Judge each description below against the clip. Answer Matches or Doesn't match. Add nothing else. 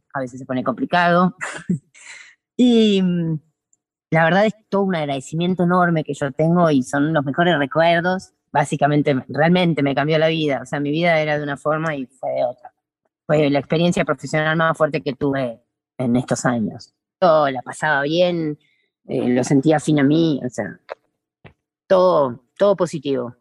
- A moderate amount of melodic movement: Matches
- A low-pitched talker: Doesn't match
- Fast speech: Doesn't match